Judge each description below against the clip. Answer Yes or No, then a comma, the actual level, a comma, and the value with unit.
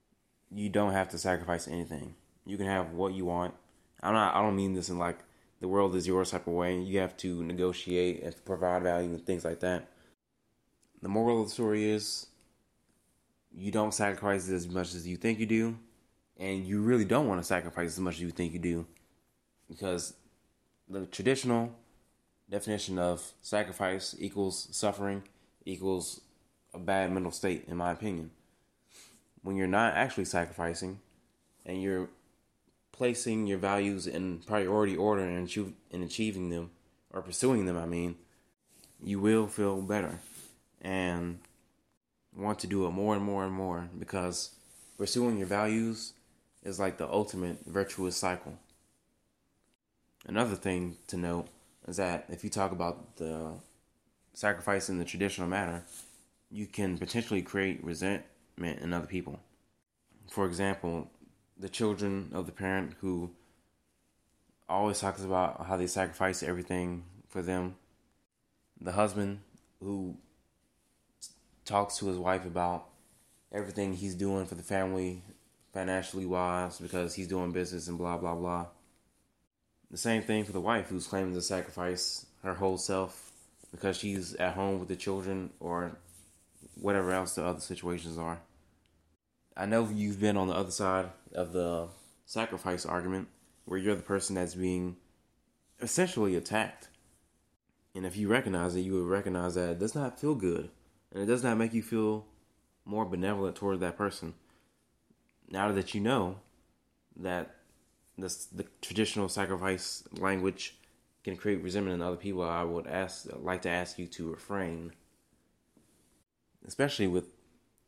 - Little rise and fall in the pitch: Yes, narrow, 2.3 semitones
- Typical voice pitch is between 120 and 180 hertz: No, very low, 95 Hz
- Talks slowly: No, average, 150 wpm